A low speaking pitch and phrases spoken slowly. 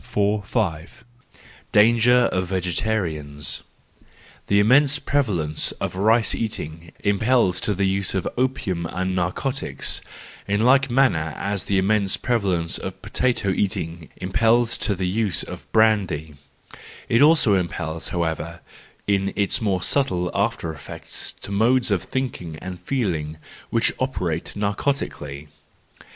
Yes: low, 100 Hz; slow, 125 wpm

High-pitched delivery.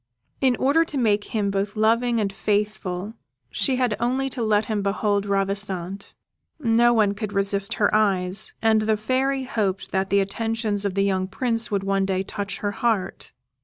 Yes: high, 210 Hz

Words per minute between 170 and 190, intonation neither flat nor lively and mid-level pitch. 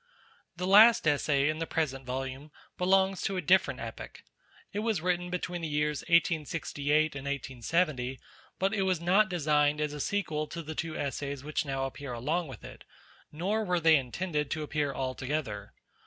Yes: average, 175 wpm; average, 4.1 semitones; medium, 155 Hz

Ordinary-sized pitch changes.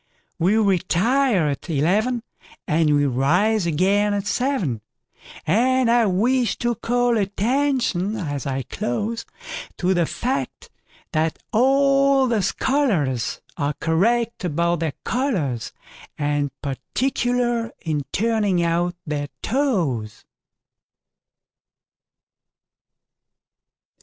No: wide, 7.5 semitones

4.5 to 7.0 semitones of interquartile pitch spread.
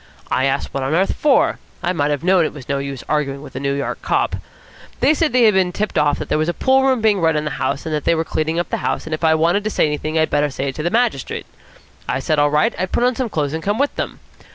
Yes: average, 5.2 semitones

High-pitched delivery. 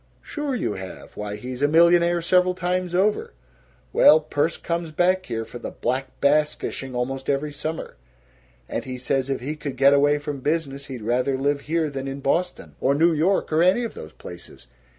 No: medium, 145 Hz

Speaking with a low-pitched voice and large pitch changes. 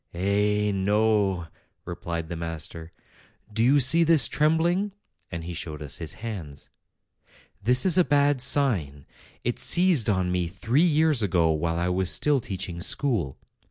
Yes: low, 105 Hz; wide, 8.6 semitones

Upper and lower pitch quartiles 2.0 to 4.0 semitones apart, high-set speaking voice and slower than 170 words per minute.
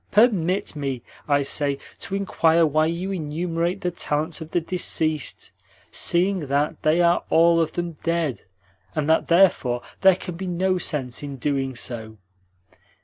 No: average, 3.4 semitones; medium, 165 Hz; average, 150 wpm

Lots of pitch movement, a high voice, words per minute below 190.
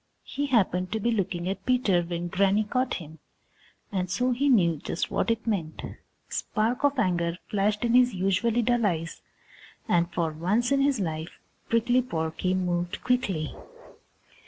Yes: wide, 5.7 semitones; high, 195 Hz; average, 160 wpm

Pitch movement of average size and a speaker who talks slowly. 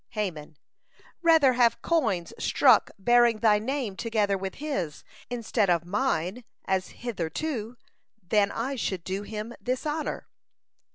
Yes: average, 4.7 semitones; slow, 125 wpm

